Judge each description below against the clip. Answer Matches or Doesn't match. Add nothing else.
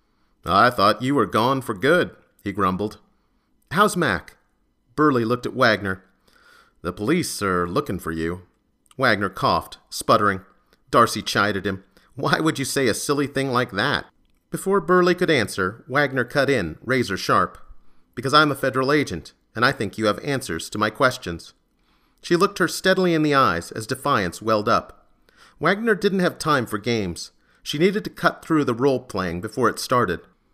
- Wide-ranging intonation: Matches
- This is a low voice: Matches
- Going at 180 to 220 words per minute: Doesn't match